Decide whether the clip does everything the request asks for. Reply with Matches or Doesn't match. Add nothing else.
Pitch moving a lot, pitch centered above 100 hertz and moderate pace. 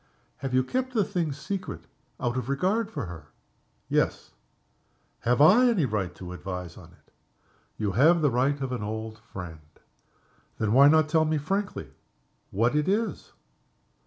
Matches